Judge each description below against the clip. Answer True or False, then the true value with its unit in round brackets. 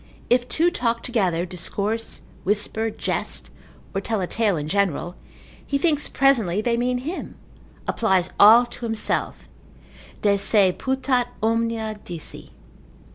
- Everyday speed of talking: False (130 wpm)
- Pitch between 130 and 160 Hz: False (225 Hz)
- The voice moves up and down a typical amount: True (3.8 semitones)